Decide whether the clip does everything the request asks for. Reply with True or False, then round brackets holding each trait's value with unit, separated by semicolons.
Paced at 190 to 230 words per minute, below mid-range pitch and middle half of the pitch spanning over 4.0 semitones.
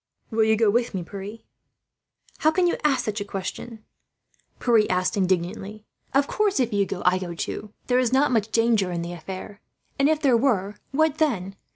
False (200 wpm; 215 Hz; 5.0 semitones)